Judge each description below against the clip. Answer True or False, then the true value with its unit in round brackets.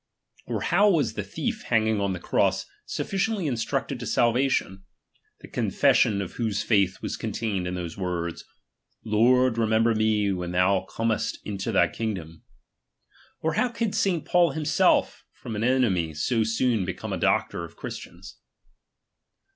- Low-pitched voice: True (110 Hz)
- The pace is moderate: True (145 wpm)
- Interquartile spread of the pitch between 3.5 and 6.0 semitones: True (5.1 semitones)